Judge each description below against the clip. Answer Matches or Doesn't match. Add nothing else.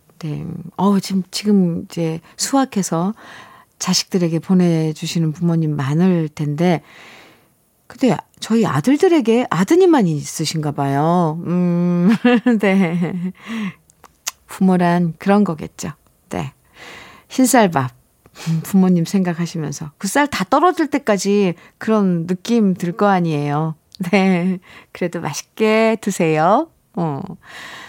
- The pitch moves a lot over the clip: Doesn't match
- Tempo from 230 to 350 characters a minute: Doesn't match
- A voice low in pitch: Doesn't match